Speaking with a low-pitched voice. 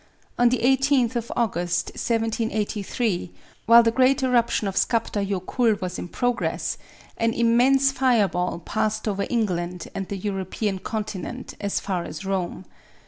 No: high, 220 Hz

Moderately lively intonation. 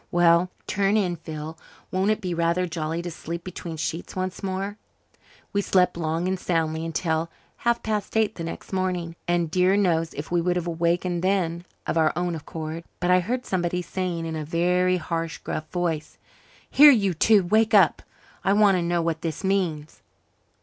No: narrow, 2.3 semitones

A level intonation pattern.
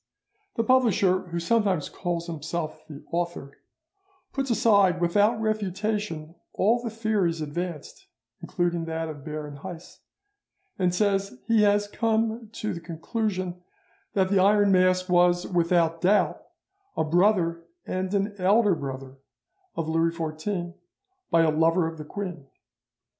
No: average, 3.8 semitones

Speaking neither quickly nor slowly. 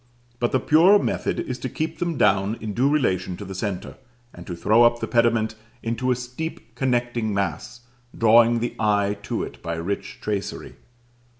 Yes: average, 180 wpm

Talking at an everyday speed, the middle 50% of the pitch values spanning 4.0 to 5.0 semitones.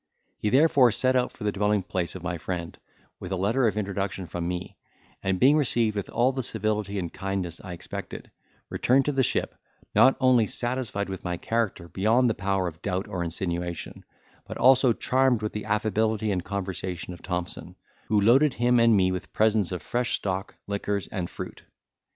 Yes: average, 185 wpm; average, 4.3 semitones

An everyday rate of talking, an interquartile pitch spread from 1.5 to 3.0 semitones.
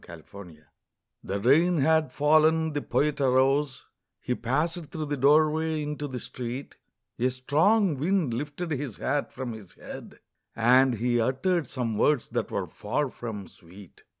No: average, 155 wpm; average, 4.4 semitones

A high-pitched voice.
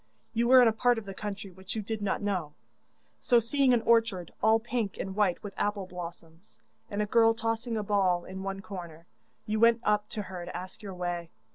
Yes: high, 205 Hz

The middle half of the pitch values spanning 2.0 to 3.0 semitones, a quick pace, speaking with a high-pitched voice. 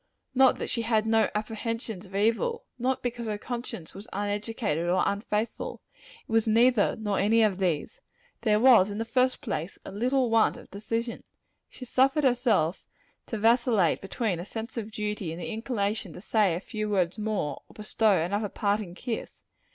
No: average, 2.7 semitones; average, 175 wpm; high, 215 Hz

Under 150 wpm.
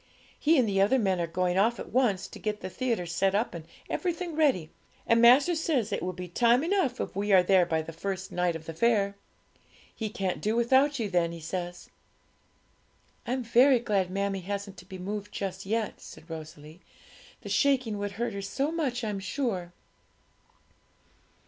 No: average, 190 wpm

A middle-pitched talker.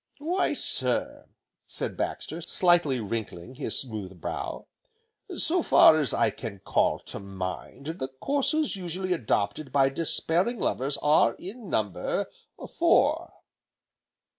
Yes: medium, 145 Hz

